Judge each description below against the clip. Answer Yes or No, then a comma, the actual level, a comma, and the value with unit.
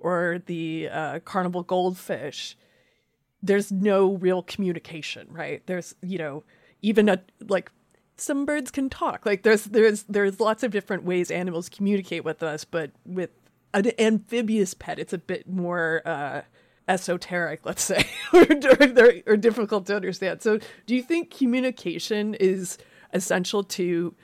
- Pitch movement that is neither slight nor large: Yes, average, 3.8 semitones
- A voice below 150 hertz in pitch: No, high, 190 Hz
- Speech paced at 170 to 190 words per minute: No, average, 145 wpm